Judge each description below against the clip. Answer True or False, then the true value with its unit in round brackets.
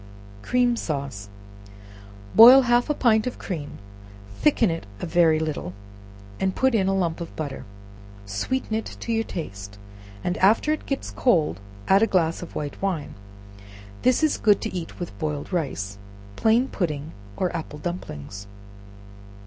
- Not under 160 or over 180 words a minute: False (150 wpm)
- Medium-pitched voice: True (175 Hz)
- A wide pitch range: True (7.1 semitones)